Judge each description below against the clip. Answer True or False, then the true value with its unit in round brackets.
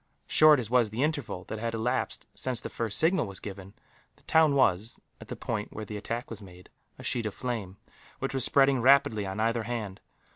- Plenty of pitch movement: False (4.0 semitones)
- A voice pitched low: True (115 Hz)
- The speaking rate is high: True (210 wpm)